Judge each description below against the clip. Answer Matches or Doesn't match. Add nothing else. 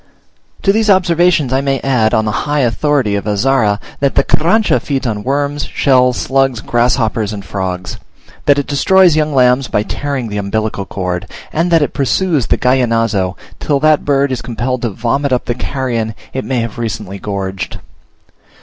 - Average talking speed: Matches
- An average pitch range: Matches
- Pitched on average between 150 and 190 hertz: Doesn't match